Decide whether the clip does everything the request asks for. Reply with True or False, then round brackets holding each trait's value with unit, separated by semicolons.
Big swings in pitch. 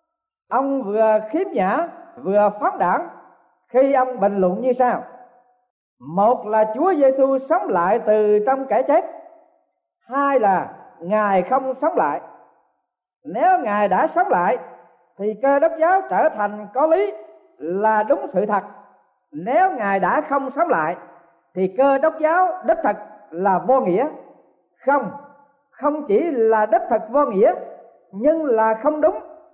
True (7.2 semitones)